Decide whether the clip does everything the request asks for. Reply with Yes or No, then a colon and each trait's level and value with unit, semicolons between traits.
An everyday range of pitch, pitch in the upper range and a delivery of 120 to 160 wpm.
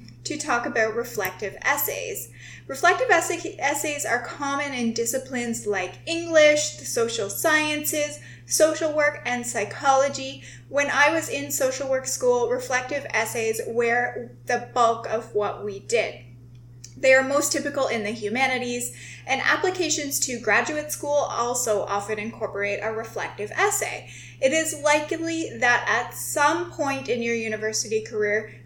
No: wide, 6.1 semitones; very high, 260 Hz; average, 140 wpm